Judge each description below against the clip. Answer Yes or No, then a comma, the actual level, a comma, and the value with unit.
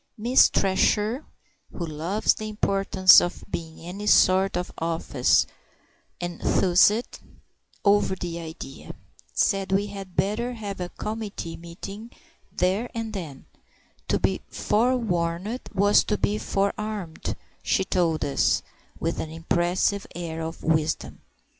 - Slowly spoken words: Yes, slow, 120 wpm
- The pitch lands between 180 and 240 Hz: Yes, high, 190 Hz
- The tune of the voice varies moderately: Yes, average, 3.7 semitones